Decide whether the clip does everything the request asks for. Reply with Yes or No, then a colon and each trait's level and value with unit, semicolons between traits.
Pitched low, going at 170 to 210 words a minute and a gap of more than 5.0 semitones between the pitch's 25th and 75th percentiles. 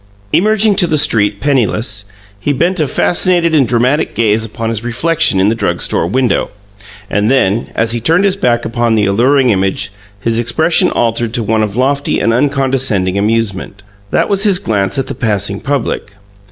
Yes: low, 115 Hz; average, 180 wpm; wide, 5.4 semitones